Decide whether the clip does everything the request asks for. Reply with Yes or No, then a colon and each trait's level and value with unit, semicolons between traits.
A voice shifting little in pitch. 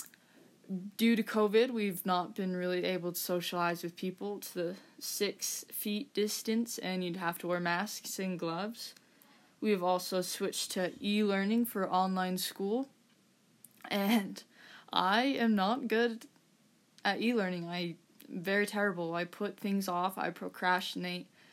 No: average, 3.6 semitones